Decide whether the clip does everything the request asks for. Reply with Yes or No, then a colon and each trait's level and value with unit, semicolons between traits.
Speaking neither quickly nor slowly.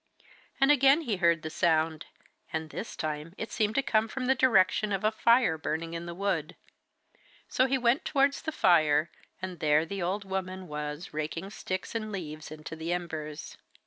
Yes: average, 180 wpm